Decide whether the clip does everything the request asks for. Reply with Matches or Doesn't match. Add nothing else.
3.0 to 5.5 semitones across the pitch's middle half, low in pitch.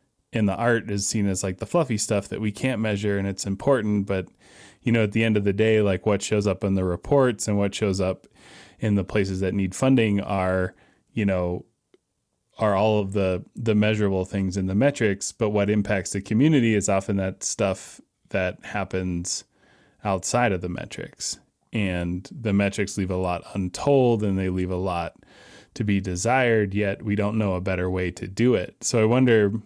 Doesn't match